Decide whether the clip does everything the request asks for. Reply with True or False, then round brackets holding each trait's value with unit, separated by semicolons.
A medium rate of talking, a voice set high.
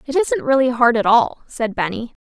False (215 wpm; 250 Hz)